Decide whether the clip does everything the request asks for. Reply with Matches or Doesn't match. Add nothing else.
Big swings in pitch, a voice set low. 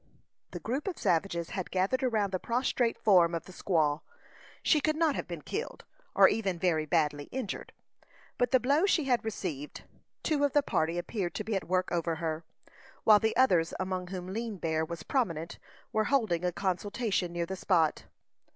Doesn't match